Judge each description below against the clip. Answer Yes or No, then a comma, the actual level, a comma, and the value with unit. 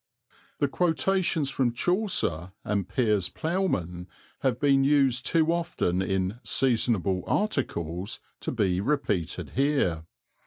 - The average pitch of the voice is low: Yes, low, 120 Hz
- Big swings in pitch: Yes, wide, 8.1 semitones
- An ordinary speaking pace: No, slow, 110 wpm